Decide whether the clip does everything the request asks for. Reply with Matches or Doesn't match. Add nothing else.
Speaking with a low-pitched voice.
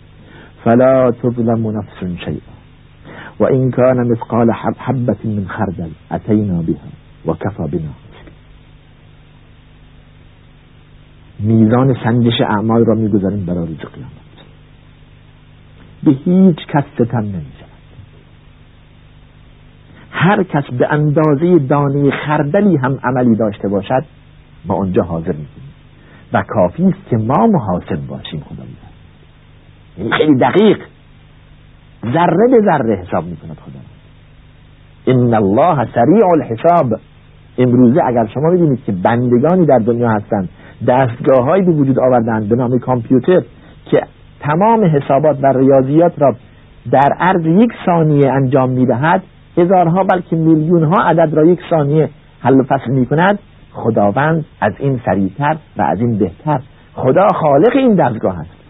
Matches